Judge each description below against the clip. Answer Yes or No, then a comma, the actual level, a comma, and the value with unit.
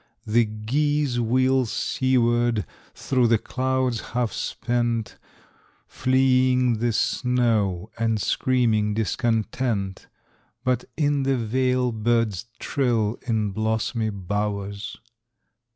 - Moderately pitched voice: No, low, 120 Hz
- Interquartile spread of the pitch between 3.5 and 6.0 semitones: No, average, 2.9 semitones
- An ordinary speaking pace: No, slow, 90 wpm